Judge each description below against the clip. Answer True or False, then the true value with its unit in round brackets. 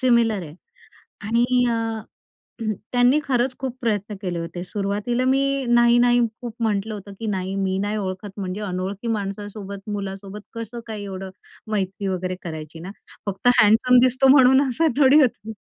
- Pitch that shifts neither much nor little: True (3.8 semitones)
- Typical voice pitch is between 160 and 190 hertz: False (210 Hz)